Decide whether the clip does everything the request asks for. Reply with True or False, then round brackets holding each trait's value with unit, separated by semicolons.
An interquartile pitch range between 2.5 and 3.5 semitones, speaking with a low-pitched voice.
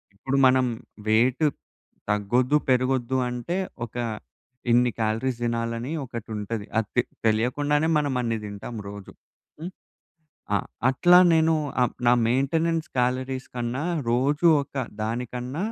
True (2.9 semitones; 125 Hz)